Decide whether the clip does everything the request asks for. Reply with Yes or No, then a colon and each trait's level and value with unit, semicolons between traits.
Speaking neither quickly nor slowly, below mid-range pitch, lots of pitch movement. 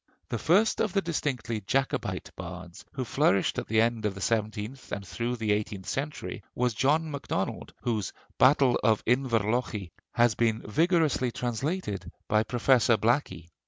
No: average, 150 wpm; low, 120 Hz; average, 4.3 semitones